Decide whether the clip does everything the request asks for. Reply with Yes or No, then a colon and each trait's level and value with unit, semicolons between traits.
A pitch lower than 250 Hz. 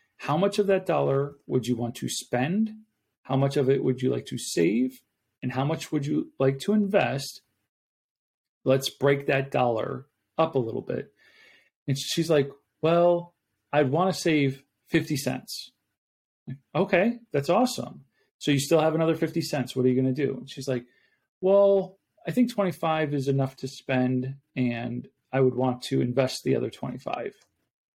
Yes: medium, 140 Hz